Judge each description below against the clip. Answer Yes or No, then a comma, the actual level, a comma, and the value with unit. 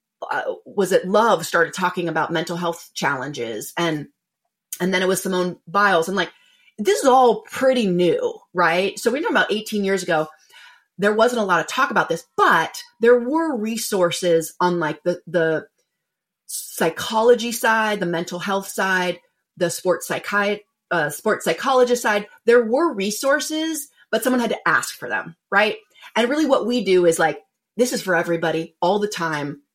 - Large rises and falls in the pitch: Yes, wide, 5.9 semitones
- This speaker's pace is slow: No, average, 175 wpm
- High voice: Yes, high, 195 Hz